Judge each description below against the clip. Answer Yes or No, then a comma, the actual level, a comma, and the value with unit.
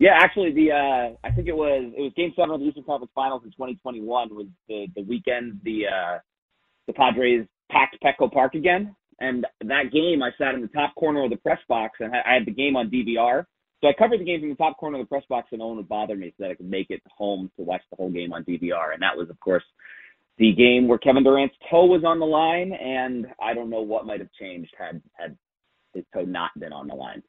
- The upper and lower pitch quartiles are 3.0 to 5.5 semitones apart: Yes, average, 4.8 semitones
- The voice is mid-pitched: No, low, 130 Hz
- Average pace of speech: No, fast, 265 wpm